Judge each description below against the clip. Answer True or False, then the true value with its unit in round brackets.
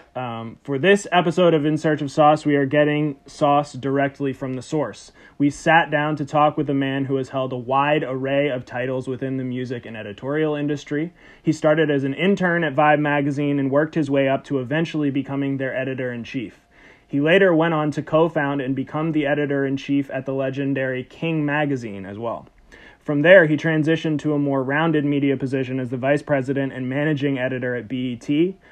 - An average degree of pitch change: False (2.3 semitones)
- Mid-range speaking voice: True (145 Hz)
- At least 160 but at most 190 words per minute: False (205 wpm)